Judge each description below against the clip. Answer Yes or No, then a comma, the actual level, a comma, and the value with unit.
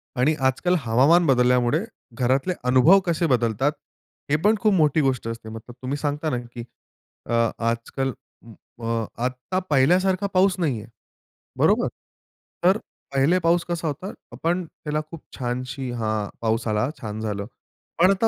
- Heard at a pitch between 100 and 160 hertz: Yes, low, 135 Hz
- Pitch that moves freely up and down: Yes, wide, 5.9 semitones